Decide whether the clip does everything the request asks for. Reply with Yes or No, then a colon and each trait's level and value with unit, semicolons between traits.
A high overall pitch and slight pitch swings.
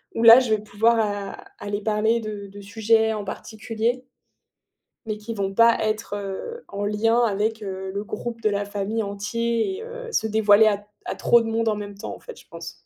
Yes: high, 215 Hz; narrow, 2.1 semitones